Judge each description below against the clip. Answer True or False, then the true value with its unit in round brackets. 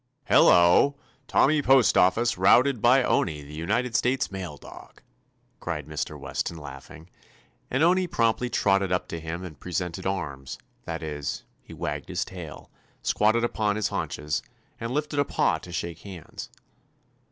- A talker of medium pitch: False (95 Hz)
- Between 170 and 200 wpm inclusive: False (145 wpm)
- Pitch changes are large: True (6.6 semitones)